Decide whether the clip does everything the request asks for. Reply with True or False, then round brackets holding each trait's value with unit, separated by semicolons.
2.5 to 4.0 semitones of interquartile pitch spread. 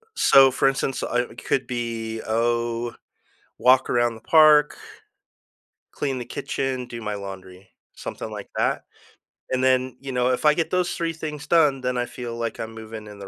True (2.8 semitones)